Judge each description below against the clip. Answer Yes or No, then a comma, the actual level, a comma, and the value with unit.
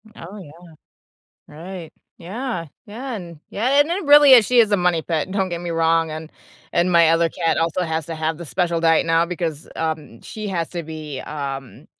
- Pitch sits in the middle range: Yes, medium, 170 Hz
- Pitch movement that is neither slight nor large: Yes, average, 3.2 semitones